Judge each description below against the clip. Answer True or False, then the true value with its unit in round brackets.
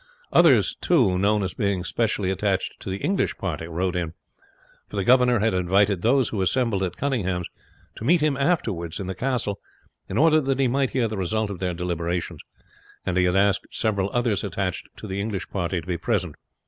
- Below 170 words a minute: False (200 wpm)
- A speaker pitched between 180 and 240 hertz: False (100 Hz)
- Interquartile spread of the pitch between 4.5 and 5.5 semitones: True (4.8 semitones)